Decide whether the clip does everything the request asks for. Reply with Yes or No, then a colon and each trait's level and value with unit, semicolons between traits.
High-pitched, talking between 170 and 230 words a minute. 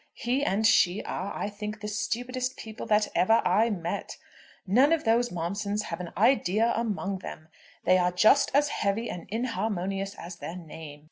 Yes: high, 205 Hz; average, 175 wpm